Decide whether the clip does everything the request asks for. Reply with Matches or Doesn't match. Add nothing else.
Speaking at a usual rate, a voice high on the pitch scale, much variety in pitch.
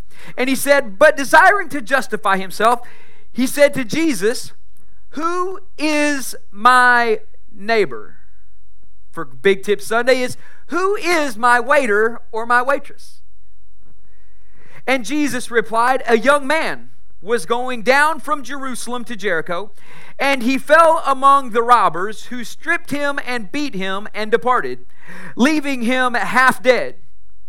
Doesn't match